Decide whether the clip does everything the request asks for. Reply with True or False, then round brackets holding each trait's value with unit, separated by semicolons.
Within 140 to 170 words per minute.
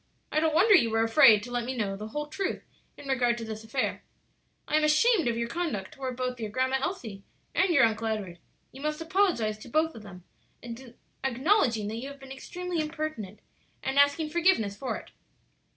False (200 wpm)